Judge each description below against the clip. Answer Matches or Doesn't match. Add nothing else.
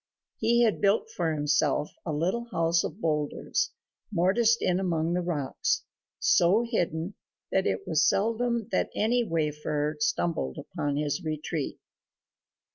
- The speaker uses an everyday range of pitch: Doesn't match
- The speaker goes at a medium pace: Doesn't match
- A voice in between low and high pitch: Matches